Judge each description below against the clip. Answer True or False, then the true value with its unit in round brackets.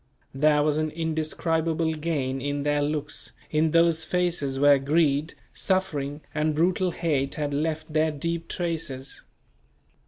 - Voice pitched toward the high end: False (155 Hz)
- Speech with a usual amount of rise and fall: False (2.2 semitones)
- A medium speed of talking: False (130 wpm)